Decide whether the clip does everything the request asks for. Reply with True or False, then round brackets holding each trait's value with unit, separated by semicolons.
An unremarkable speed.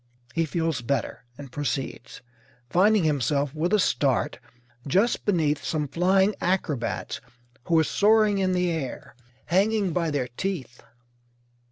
False (125 wpm)